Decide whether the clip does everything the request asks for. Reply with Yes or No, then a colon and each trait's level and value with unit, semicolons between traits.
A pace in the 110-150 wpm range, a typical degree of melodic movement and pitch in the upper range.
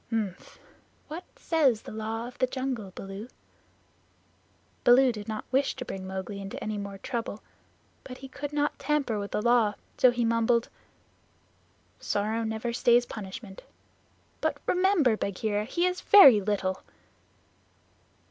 Yes: average, 140 wpm; average, 3.9 semitones; high, 230 Hz